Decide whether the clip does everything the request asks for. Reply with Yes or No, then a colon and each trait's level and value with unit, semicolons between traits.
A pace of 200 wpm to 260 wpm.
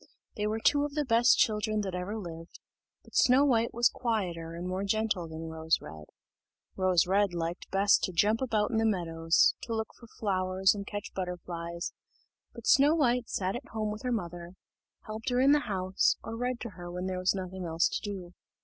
Yes: fast, 205 wpm